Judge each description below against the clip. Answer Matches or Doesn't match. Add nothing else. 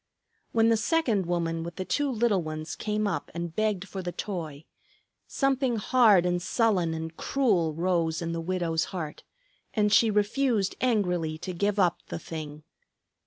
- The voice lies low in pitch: Doesn't match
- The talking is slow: Doesn't match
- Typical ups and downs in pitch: Matches